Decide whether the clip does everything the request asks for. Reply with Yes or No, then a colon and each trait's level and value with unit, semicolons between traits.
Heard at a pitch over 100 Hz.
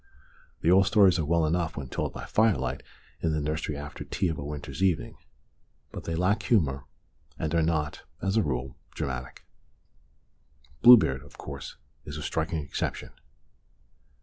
No: very low, 80 Hz